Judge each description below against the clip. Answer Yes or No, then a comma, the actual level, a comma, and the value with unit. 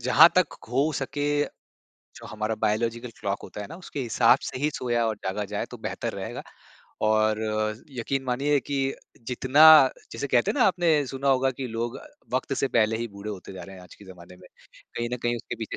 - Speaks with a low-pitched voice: Yes, low, 120 Hz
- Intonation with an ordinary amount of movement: Yes, average, 4.0 semitones